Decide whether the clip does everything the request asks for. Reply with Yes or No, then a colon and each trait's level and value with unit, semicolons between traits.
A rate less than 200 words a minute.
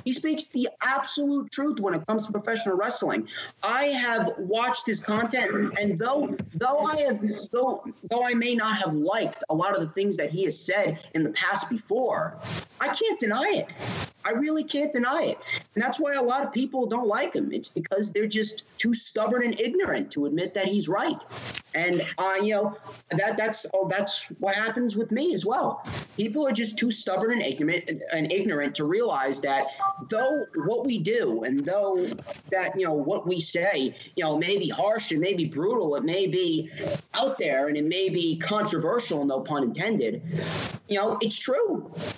Yes: average, 190 wpm